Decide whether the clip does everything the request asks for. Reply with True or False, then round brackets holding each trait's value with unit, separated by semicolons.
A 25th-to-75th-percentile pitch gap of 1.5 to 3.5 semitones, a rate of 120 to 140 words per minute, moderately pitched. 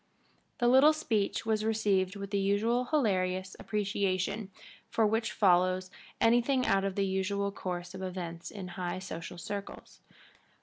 False (2.9 semitones; 135 wpm; 200 Hz)